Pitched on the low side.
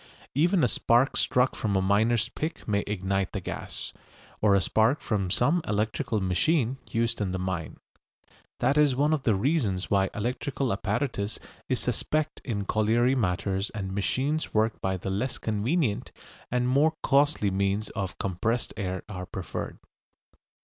Yes: low, 110 Hz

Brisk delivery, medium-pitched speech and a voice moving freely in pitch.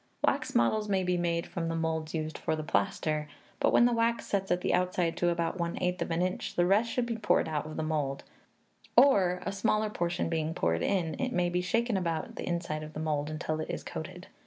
No: fast, 235 wpm; medium, 175 Hz; average, 3.3 semitones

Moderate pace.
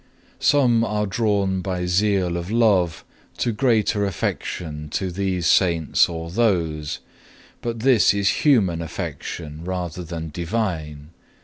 No: slow, 125 wpm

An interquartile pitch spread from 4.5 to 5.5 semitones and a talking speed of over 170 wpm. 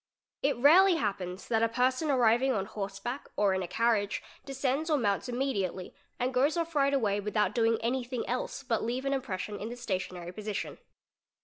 Yes: average, 4.8 semitones; average, 190 wpm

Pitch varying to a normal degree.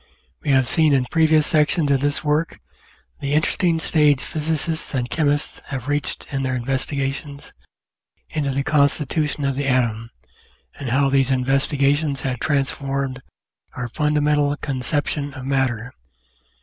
No: narrow, 2.0 semitones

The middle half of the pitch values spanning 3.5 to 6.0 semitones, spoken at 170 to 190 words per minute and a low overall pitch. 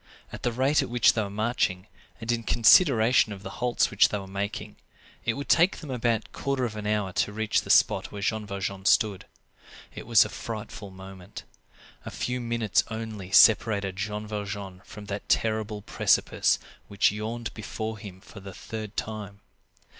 No: narrow, 2.4 semitones; average, 180 wpm; low, 105 Hz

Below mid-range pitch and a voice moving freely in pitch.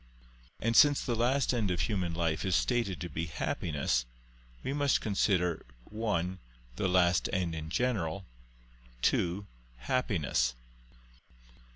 Yes: very low, 95 Hz; wide, 5.7 semitones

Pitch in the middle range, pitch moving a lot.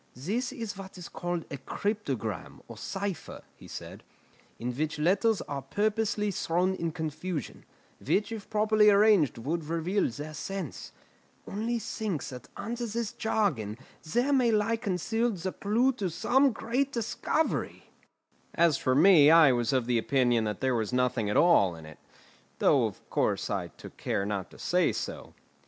Yes: medium, 180 Hz; wide, 8.0 semitones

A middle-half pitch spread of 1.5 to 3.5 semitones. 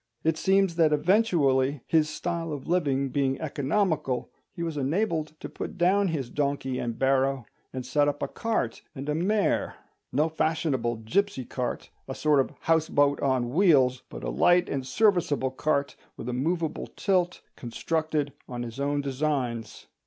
No: average, 4.0 semitones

